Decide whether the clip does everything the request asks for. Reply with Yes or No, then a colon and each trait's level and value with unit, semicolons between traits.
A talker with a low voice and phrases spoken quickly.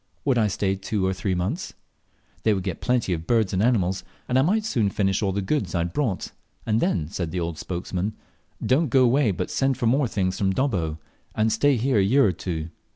Yes: low, 100 Hz; fast, 230 wpm